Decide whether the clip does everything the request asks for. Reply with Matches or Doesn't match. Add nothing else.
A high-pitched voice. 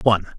Doesn't match